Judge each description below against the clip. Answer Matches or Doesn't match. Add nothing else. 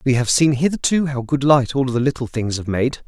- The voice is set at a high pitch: Doesn't match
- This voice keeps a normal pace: Doesn't match